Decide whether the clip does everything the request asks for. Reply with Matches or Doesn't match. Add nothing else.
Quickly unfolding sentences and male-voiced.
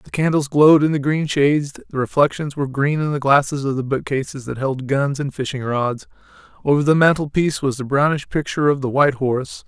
Matches